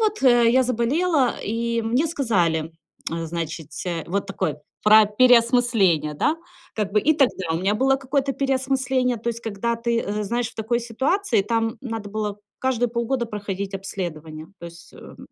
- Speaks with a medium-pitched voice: No, high, 230 Hz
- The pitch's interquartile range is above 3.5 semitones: Yes, average, 4.5 semitones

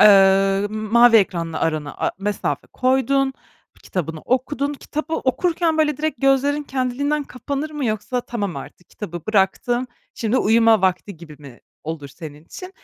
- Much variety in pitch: Yes, wide, 6.5 semitones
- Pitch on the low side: No, high, 225 Hz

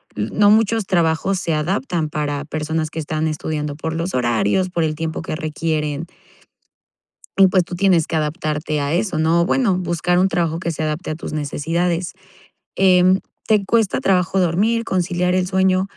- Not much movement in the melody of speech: No, average, 3.2 semitones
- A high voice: No, medium, 170 Hz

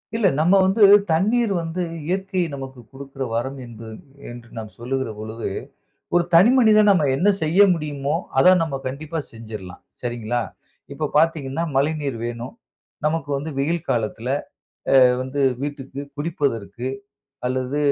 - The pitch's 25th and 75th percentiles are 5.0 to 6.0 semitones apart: Yes, average, 5.3 semitones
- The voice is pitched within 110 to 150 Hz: Yes, medium, 140 Hz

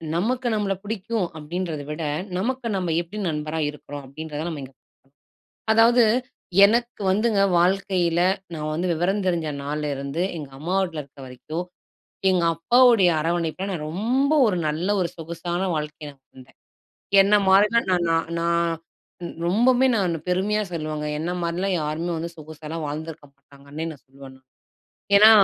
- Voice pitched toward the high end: No, medium, 170 Hz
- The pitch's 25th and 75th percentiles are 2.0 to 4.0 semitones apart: No, average, 4.4 semitones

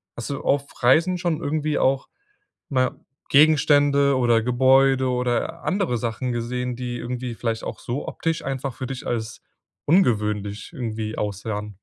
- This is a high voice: No, low, 125 Hz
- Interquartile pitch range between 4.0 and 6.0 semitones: No, average, 3.3 semitones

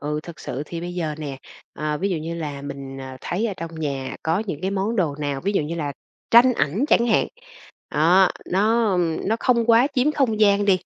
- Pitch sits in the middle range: Yes, medium, 175 Hz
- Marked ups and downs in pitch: Yes, wide, 5.9 semitones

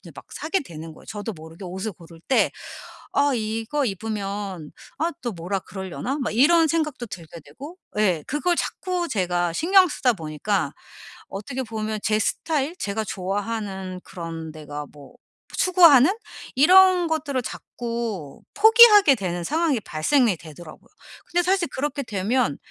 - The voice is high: Yes, high, 220 Hz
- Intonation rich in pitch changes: Yes, wide, 8.5 semitones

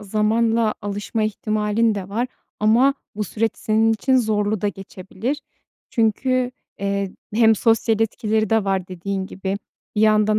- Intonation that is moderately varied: No, narrow, 2.0 semitones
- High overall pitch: Yes, high, 215 Hz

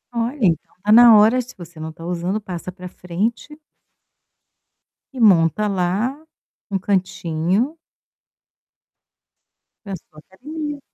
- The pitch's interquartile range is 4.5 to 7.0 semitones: Yes, average, 5.1 semitones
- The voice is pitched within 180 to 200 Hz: Yes, high, 195 Hz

